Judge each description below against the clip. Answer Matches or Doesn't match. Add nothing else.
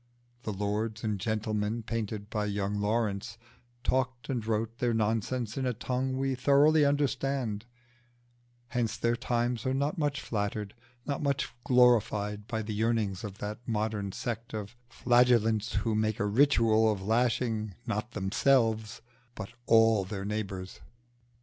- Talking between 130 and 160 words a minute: Matches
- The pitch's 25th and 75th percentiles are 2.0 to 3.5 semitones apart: Matches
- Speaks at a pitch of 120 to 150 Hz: Doesn't match